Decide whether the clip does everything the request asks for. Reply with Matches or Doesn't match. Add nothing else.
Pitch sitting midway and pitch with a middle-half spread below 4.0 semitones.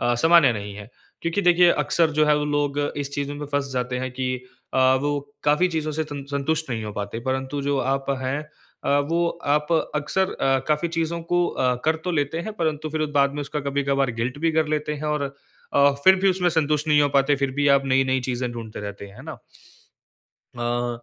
Matches